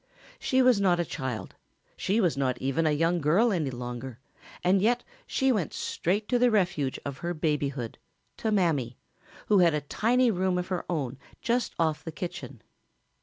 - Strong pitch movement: Yes, wide, 6.4 semitones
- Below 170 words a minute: No, average, 175 wpm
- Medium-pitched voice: Yes, medium, 170 Hz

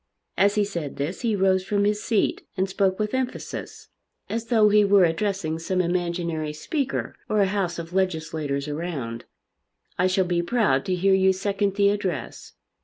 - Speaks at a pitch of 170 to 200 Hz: Yes, high, 190 Hz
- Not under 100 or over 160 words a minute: No, average, 175 wpm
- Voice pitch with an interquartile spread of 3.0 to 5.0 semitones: Yes, average, 3.3 semitones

